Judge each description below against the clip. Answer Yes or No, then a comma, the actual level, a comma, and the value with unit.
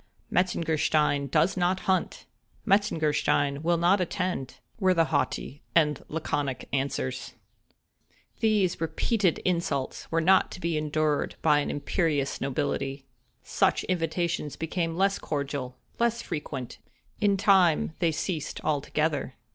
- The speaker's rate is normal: No, slow, 110 wpm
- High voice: No, medium, 160 Hz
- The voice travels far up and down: No, average, 3.9 semitones